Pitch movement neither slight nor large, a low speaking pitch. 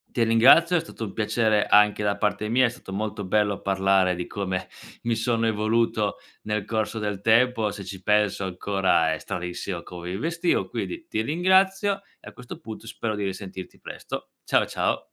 Yes: average, 3.1 semitones; low, 105 Hz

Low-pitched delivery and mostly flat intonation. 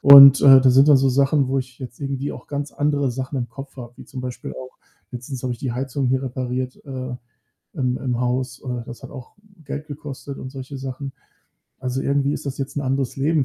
Yes: low, 130 Hz; narrow, 1.5 semitones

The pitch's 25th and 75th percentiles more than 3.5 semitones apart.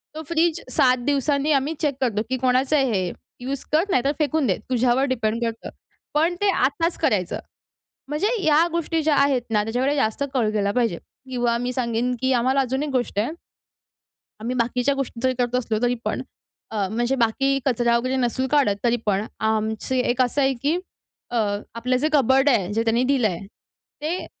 No: average, 3.2 semitones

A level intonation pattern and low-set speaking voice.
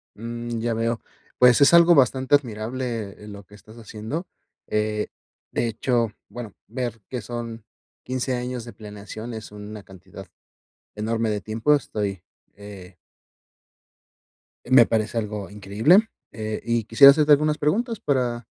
No: average, 3.0 semitones; low, 115 Hz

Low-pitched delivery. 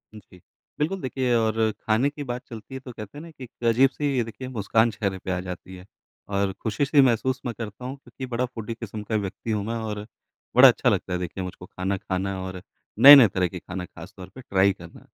Yes: low, 110 Hz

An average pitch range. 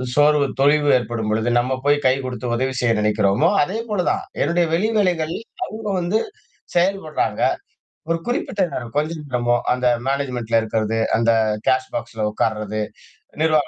No: wide, 6.2 semitones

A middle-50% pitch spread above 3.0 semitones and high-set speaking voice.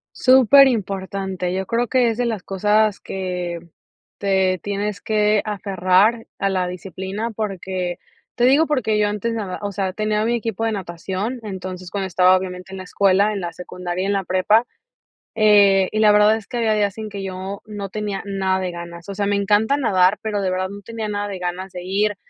No: narrow, 2.4 semitones; high, 200 Hz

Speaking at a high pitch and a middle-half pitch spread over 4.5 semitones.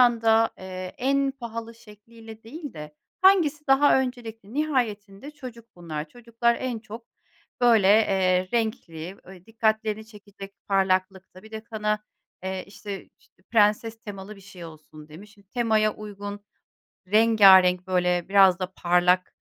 No: high, 210 Hz; average, 3.5 semitones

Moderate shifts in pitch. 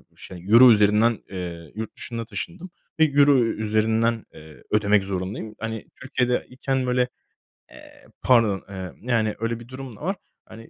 Yes: average, 3.3 semitones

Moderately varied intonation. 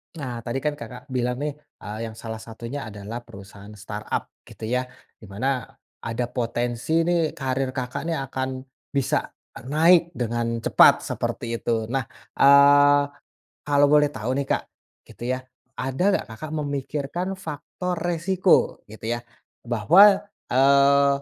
Yes: average, 3.7 semitones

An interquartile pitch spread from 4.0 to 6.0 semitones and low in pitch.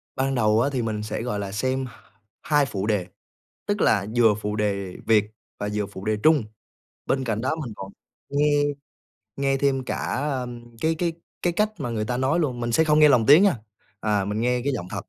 Yes: average, 5.0 semitones; low, 120 Hz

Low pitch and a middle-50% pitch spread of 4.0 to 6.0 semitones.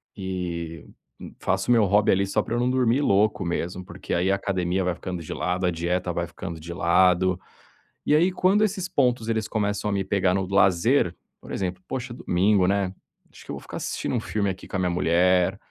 No: very low, 95 Hz; average, 2.9 semitones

